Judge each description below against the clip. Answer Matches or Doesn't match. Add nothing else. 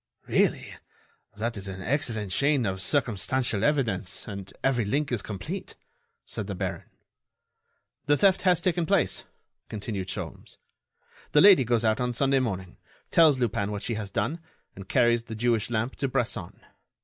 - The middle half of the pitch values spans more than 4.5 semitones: Matches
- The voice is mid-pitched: Doesn't match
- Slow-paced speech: Doesn't match